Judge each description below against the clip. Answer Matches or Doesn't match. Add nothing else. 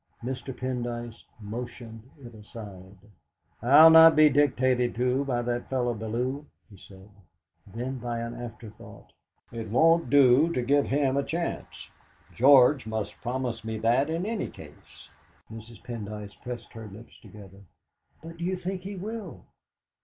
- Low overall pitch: Matches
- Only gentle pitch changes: Doesn't match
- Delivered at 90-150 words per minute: Matches